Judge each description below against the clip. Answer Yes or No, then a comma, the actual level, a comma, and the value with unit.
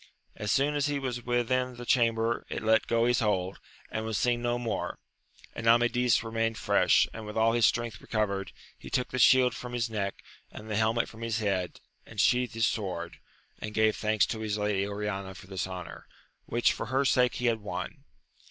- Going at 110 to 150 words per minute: No, average, 200 wpm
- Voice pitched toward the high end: No, low, 115 Hz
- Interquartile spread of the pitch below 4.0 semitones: Yes, narrow, 2.5 semitones